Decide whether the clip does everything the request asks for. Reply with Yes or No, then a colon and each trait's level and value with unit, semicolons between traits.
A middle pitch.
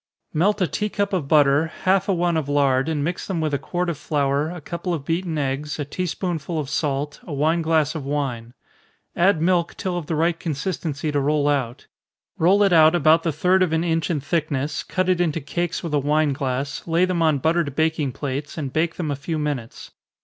Yes: medium, 155 Hz